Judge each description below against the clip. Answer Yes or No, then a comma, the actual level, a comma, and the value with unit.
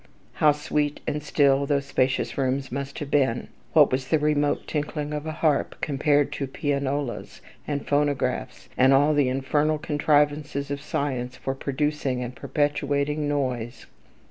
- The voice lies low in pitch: No, medium, 145 Hz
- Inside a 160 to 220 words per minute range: No, average, 145 wpm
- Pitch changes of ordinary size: No, narrow, 1.6 semitones